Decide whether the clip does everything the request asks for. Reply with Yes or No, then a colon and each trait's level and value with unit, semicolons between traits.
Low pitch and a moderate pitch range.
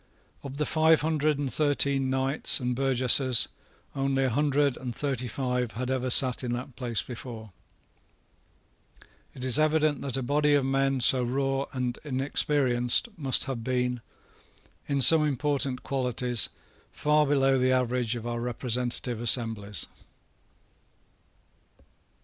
No: low, 130 Hz; narrow, 2.2 semitones